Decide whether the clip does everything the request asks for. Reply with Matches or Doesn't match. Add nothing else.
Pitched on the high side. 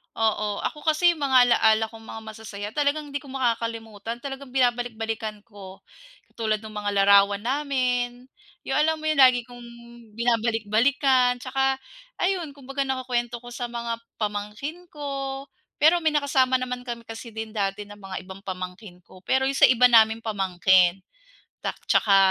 Matches